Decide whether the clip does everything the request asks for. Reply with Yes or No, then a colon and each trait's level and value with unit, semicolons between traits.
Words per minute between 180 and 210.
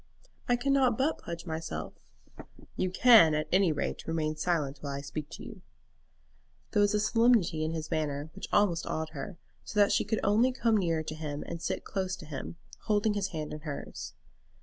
Yes: average, 195 wpm